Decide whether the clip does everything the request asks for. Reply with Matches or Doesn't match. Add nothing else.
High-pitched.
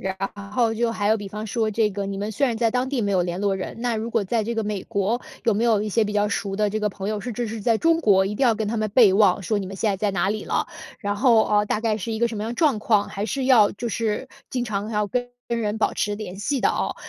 Matches